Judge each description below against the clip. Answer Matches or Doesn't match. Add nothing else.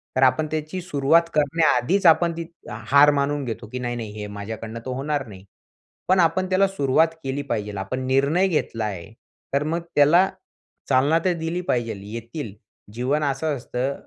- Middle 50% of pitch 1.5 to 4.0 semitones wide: Doesn't match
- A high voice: Doesn't match